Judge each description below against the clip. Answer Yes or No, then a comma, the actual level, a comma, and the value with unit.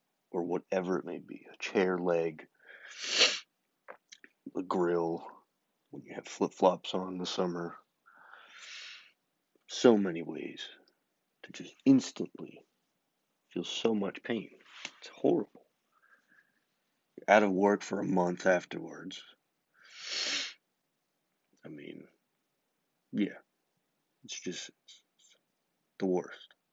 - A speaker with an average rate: No, slow, 110 wpm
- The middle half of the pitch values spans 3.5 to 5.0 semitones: No, average, 2.9 semitones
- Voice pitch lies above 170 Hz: No, very low, 90 Hz